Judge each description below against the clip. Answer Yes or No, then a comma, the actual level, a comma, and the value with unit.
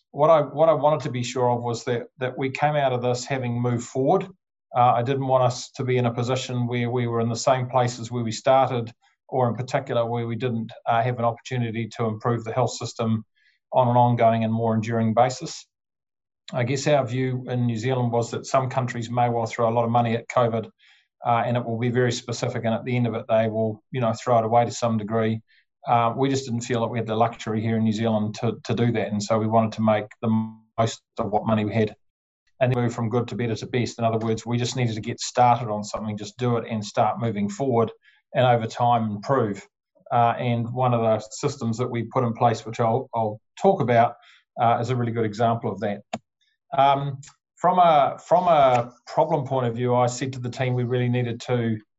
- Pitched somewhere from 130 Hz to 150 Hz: No, low, 120 Hz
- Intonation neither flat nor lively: No, narrow, 1.8 semitones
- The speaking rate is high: Yes, fast, 240 wpm